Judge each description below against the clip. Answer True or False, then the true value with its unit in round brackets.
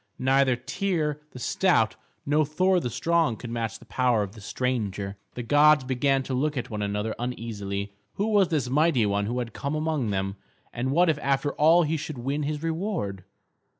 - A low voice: True (130 Hz)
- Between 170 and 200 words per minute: True (190 wpm)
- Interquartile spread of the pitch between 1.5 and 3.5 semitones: False (5.2 semitones)